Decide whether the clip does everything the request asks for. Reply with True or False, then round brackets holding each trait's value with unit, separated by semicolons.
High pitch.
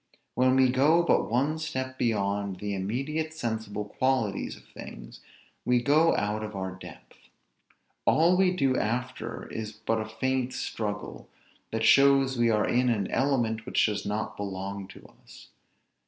False (120 Hz)